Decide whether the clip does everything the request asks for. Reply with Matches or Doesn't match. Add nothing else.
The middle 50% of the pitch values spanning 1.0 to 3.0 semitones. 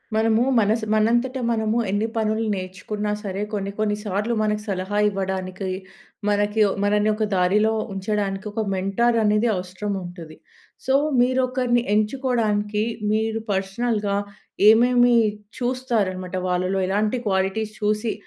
Matches